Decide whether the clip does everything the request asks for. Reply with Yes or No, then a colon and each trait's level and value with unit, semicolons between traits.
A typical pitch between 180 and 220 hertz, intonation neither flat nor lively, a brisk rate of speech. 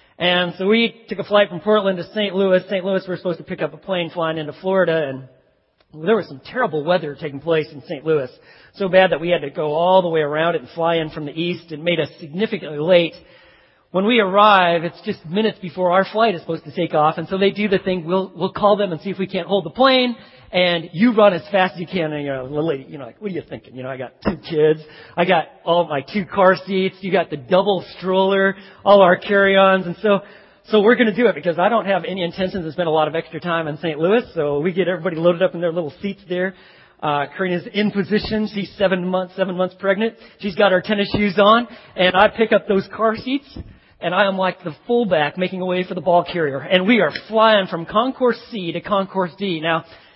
Yes: medium, 185 Hz; average, 3.2 semitones; fast, 255 wpm